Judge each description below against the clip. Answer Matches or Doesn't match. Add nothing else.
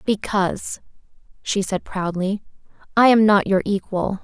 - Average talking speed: Doesn't match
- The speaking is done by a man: Doesn't match